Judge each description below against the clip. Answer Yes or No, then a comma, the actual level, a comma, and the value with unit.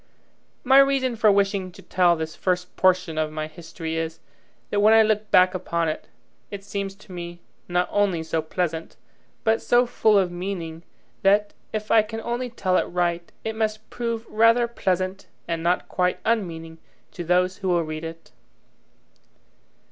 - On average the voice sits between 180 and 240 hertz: Yes, medium, 185 Hz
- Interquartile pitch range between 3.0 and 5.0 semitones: Yes, average, 4.1 semitones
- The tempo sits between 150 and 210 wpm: Yes, average, 170 wpm